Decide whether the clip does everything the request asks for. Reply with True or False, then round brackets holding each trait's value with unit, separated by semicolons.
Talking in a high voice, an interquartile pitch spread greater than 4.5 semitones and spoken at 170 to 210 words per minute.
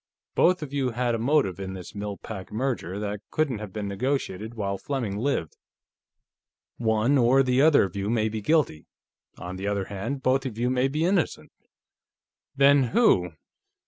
False (115 Hz; 5.2 semitones; 175 wpm)